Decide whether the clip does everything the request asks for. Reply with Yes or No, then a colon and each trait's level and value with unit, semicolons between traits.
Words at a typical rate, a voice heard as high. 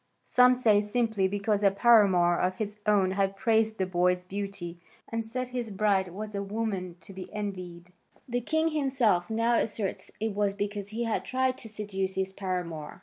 Yes: average, 180 wpm; high, 205 Hz